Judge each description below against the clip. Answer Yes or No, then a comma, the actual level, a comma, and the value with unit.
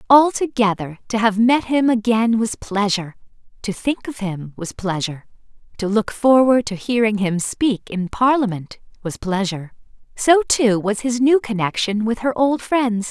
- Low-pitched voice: No, high, 220 Hz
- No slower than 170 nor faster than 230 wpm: No, average, 160 wpm